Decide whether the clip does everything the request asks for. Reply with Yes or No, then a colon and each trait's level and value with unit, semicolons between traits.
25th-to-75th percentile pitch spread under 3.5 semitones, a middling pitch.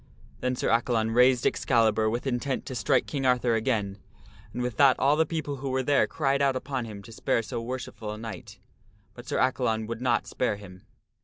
No: average, 2.9 semitones; low, 125 Hz